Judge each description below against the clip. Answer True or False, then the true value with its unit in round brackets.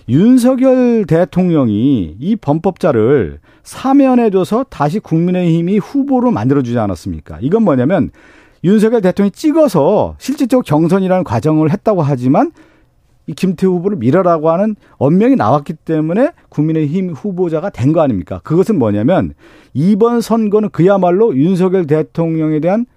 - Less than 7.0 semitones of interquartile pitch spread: True (6.1 semitones)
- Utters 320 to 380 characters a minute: True (335 characters per minute)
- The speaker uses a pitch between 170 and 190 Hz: True (185 Hz)